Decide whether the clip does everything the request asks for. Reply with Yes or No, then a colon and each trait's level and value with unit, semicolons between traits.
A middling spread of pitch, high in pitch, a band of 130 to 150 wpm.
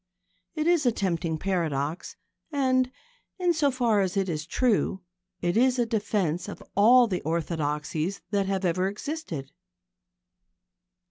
No: wide, 6.8 semitones; high, 195 Hz; slow, 135 wpm